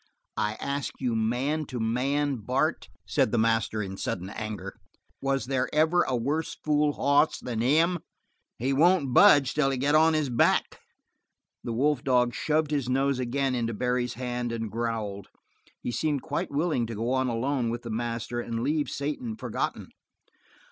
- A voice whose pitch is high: No, low, 130 Hz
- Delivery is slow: No, average, 170 wpm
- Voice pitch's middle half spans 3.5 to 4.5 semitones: Yes, average, 3.8 semitones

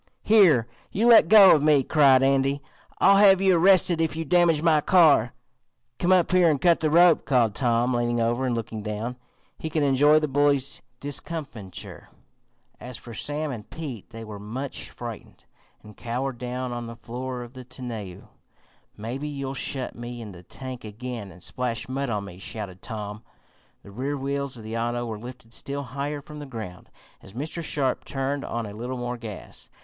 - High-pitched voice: No, low, 130 Hz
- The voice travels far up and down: No, average, 4.2 semitones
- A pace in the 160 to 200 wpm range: Yes, average, 185 wpm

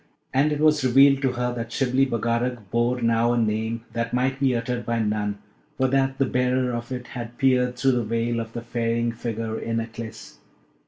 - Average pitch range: No, narrow, 1.9 semitones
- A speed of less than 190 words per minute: No, average, 200 wpm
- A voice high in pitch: No, low, 120 Hz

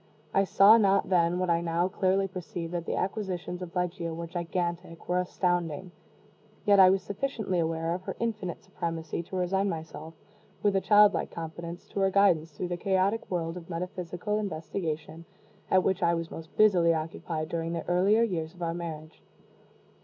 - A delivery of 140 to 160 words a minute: No, average, 175 wpm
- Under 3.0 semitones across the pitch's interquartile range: Yes, narrow, 2.5 semitones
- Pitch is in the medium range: Yes, medium, 175 Hz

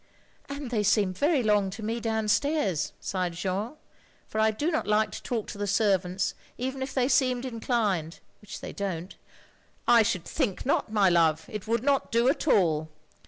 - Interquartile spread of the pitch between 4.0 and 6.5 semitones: Yes, average, 4.5 semitones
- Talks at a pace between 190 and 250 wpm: Yes, average, 195 wpm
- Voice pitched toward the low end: No, high, 215 Hz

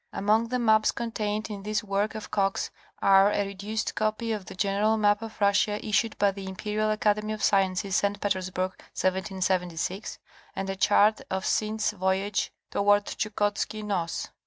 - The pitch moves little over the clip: Yes, narrow, 1.8 semitones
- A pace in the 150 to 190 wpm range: Yes, average, 160 wpm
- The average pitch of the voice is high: Yes, high, 205 Hz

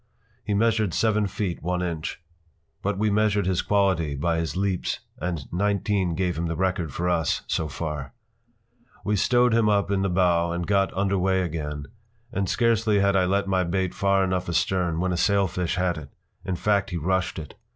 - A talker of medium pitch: No, very low, 95 Hz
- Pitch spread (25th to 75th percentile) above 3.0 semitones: No, average, 2.7 semitones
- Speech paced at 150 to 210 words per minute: Yes, average, 190 wpm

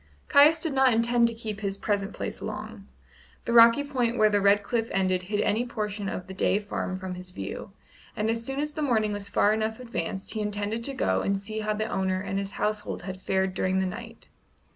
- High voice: Yes, high, 210 Hz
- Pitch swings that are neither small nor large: Yes, average, 3.1 semitones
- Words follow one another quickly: Yes, fast, 225 wpm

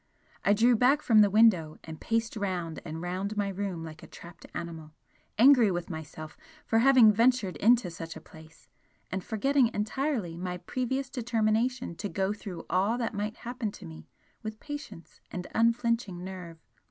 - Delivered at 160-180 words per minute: Yes, average, 165 wpm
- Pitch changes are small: No, average, 5.0 semitones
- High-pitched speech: Yes, high, 205 Hz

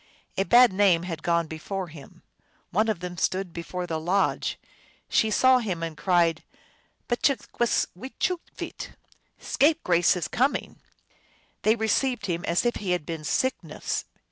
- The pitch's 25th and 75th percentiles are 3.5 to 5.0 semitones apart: No, wide, 5.4 semitones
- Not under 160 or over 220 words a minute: No, average, 145 wpm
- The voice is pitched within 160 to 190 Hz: Yes, medium, 185 Hz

